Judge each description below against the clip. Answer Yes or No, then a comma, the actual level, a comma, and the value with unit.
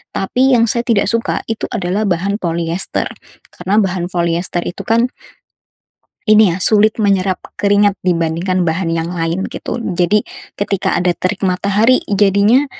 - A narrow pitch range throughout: No, average, 3.2 semitones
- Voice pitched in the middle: No, high, 195 Hz